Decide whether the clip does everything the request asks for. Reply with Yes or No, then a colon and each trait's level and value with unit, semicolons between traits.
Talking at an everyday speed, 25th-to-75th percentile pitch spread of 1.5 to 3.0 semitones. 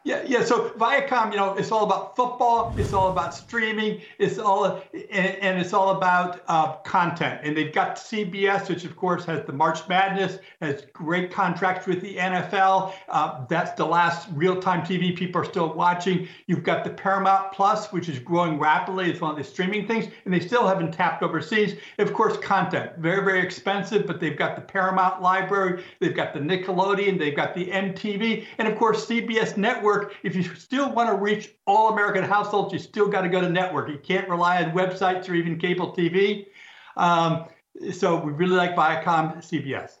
Yes: average, 195 wpm; average, 2.7 semitones